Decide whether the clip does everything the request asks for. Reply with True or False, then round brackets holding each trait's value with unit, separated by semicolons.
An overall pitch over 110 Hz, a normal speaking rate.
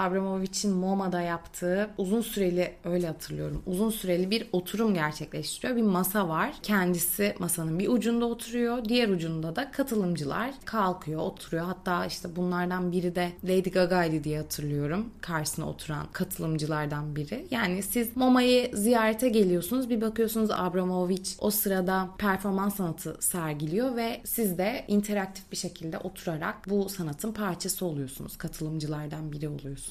True (185 Hz; 130 wpm)